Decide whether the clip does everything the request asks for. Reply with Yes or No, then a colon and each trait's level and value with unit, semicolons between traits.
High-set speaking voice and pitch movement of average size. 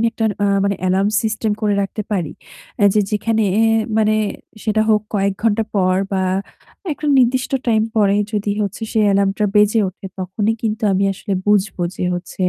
No: high, 210 Hz; narrow, 2.0 semitones